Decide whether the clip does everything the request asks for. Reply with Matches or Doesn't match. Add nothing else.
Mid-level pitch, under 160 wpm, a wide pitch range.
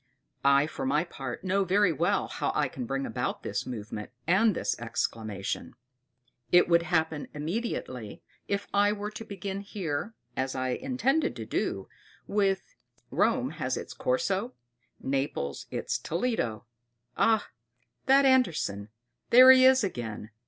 Matches